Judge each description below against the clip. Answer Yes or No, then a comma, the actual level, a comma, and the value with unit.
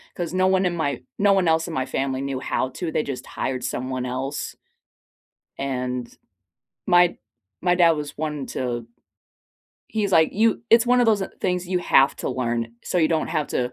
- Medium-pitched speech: Yes, medium, 155 Hz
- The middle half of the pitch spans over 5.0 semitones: Yes, wide, 5.6 semitones